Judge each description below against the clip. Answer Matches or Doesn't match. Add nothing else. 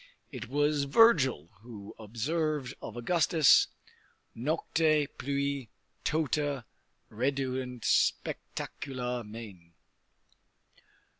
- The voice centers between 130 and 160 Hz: Matches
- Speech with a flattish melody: Doesn't match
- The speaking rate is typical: Doesn't match